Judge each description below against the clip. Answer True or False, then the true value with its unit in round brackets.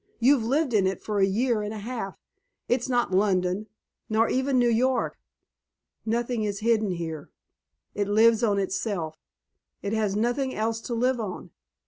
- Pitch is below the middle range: False (220 Hz)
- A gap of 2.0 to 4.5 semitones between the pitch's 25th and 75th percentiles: True (3.2 semitones)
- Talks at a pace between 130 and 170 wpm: True (160 wpm)